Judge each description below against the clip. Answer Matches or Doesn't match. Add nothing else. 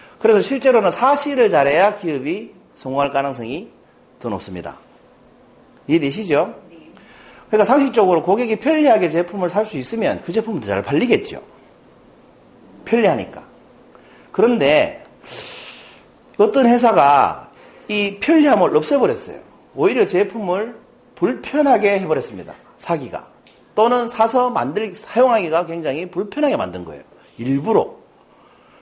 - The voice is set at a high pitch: Matches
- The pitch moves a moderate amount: Doesn't match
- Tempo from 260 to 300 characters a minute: Matches